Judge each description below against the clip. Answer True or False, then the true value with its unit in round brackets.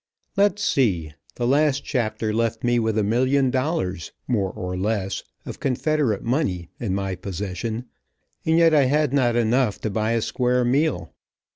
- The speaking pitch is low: True (120 Hz)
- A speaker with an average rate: True (160 wpm)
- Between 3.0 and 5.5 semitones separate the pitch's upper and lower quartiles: True (5.1 semitones)